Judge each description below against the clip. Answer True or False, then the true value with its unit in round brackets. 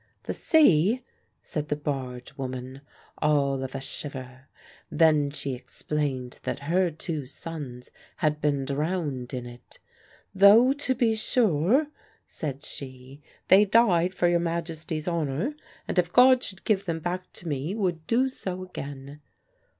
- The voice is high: False (155 Hz)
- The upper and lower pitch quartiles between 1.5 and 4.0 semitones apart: False (5.3 semitones)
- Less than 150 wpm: True (140 wpm)